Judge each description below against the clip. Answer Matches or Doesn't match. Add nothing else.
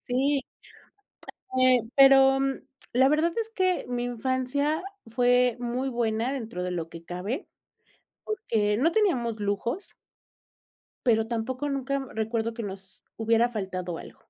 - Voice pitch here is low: Doesn't match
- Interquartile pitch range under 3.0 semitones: Doesn't match